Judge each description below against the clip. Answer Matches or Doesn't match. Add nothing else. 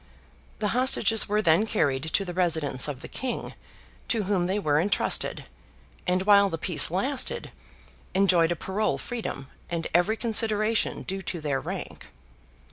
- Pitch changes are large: Doesn't match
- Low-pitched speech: Doesn't match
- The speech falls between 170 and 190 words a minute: Doesn't match